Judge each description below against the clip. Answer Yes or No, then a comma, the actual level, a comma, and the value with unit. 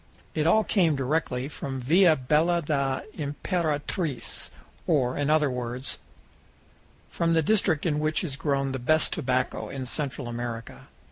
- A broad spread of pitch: No, average, 3.6 semitones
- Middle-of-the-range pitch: Yes, medium, 145 Hz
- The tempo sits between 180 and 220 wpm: No, average, 140 wpm